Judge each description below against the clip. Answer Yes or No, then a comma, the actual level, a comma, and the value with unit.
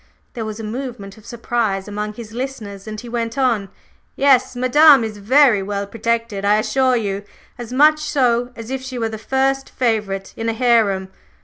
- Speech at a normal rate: Yes, average, 185 wpm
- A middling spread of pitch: Yes, average, 3.4 semitones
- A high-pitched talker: Yes, high, 230 Hz